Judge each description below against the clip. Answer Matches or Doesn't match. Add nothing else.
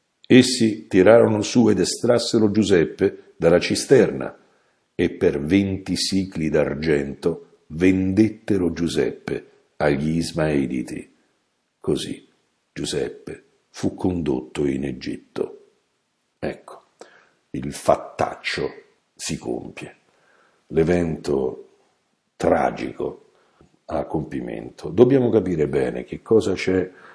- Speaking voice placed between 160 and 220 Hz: Doesn't match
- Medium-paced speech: Doesn't match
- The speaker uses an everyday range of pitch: Doesn't match